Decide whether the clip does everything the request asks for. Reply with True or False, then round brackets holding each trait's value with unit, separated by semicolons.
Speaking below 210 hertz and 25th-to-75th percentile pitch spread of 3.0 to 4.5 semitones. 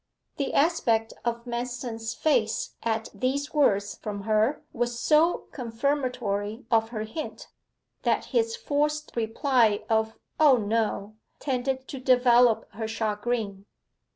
False (235 Hz; 3.5 semitones)